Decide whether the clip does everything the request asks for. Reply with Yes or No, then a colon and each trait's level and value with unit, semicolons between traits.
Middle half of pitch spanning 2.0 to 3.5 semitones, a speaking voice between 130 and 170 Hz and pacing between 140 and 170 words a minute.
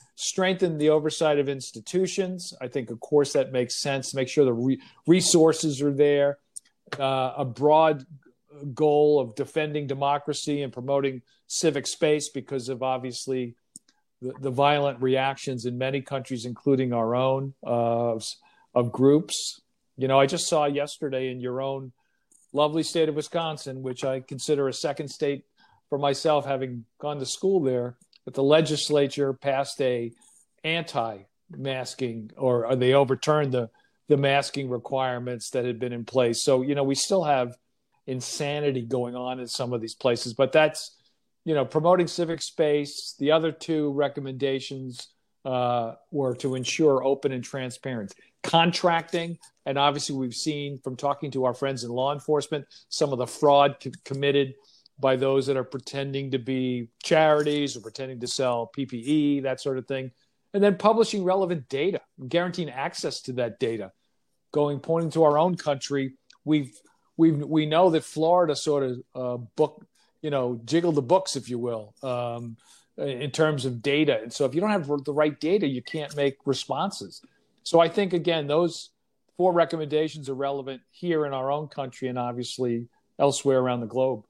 Yes: average, 3.0 semitones; medium, 140 Hz; average, 165 wpm